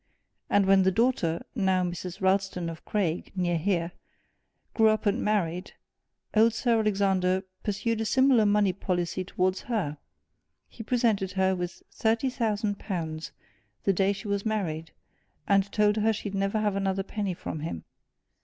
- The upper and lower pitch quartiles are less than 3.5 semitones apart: Yes, average, 2.8 semitones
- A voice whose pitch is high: Yes, high, 195 Hz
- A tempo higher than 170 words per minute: No, average, 155 wpm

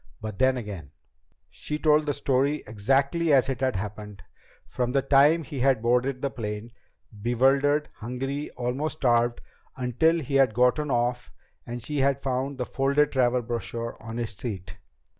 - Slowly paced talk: No, average, 160 wpm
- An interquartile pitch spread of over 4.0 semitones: No, average, 2.9 semitones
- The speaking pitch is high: No, low, 125 Hz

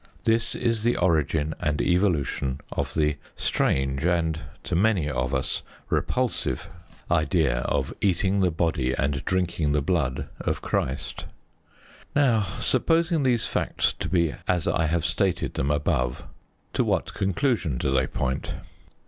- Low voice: Yes, very low, 85 Hz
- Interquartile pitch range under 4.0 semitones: No, wide, 5.5 semitones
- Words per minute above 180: No, average, 140 wpm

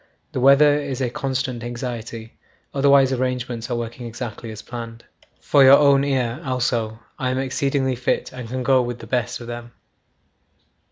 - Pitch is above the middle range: No, low, 125 Hz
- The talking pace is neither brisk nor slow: Yes, average, 165 wpm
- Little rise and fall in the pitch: Yes, narrow, 2.1 semitones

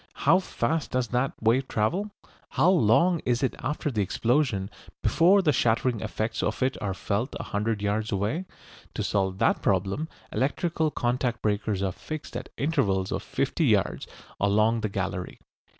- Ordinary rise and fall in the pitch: No, wide, 6.0 semitones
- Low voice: Yes, low, 115 Hz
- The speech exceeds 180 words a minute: No, average, 160 wpm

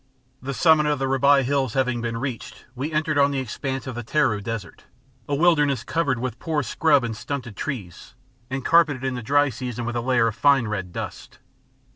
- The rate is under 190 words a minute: No, average, 200 wpm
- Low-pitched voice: Yes, low, 130 Hz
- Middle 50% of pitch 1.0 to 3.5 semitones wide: Yes, average, 3.2 semitones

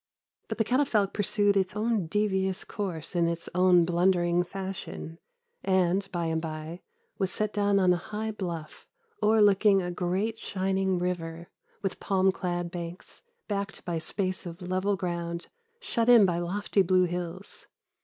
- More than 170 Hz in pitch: Yes, medium, 185 Hz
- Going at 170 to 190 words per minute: No, average, 155 wpm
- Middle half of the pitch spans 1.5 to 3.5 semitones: Yes, narrow, 2.6 semitones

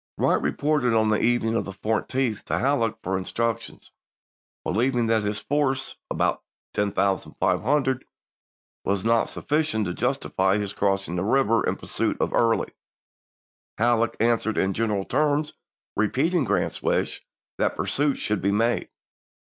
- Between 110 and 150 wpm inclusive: Yes, average, 140 wpm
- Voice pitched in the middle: No, low, 115 Hz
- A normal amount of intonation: Yes, average, 4.4 semitones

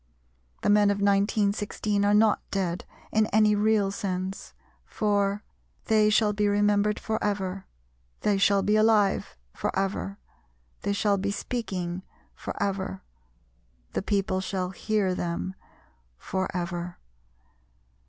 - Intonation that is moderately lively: No, narrow, 1.7 semitones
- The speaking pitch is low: No, high, 200 Hz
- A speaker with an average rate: No, slow, 125 wpm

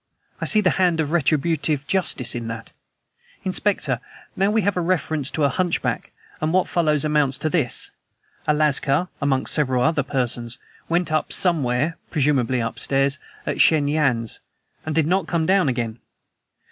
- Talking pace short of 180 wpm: Yes, average, 160 wpm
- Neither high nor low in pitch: Yes, medium, 150 Hz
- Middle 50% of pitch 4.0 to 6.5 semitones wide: Yes, average, 4.3 semitones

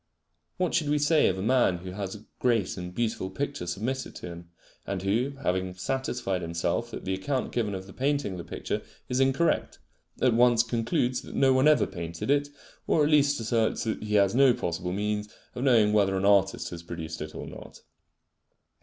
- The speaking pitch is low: Yes, low, 105 Hz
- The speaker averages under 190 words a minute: No, average, 200 wpm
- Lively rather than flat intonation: Yes, wide, 5.8 semitones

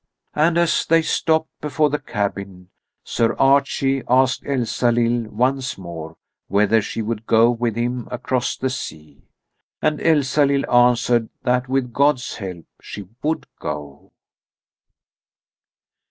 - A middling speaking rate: No, slow, 120 wpm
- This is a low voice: Yes, low, 125 Hz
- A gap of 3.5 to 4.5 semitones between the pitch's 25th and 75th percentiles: Yes, average, 4.2 semitones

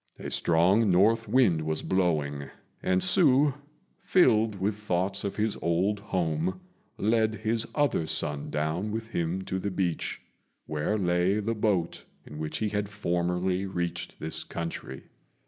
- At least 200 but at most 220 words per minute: No, average, 145 wpm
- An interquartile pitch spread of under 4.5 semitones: Yes, average, 4.1 semitones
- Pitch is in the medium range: No, very low, 95 Hz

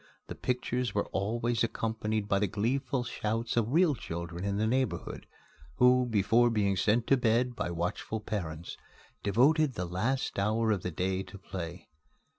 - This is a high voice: No, low, 110 Hz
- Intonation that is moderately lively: Yes, average, 3.9 semitones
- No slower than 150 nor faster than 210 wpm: Yes, average, 160 wpm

